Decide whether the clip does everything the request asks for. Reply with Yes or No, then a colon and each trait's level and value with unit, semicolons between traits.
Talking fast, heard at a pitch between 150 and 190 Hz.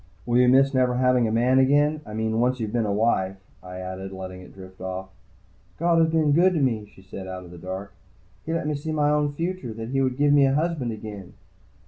No: fast, 250 wpm; low, 125 Hz